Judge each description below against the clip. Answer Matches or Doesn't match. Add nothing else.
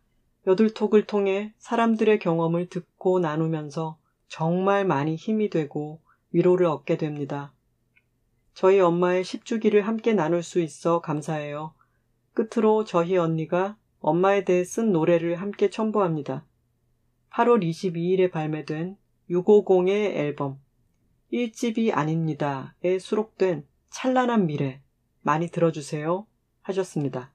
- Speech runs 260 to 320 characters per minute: Doesn't match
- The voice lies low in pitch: Doesn't match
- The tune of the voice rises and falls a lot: Doesn't match